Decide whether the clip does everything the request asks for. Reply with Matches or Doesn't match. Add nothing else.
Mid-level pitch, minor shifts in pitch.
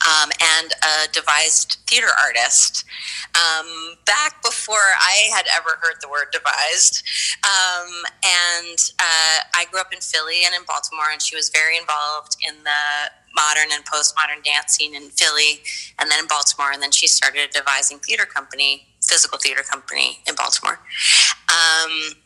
Matches